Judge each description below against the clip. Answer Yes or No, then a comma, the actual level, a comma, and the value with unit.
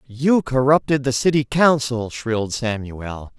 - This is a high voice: No, low, 130 Hz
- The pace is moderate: No, slow, 125 wpm